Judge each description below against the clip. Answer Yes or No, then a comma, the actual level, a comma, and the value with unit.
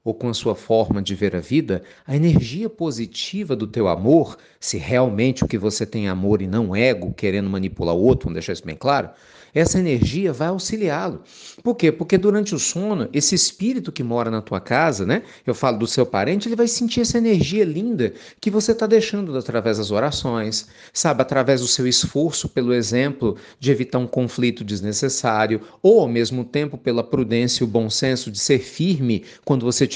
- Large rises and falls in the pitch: Yes, wide, 6.7 semitones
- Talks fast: Yes, fast, 200 wpm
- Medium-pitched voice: No, low, 130 Hz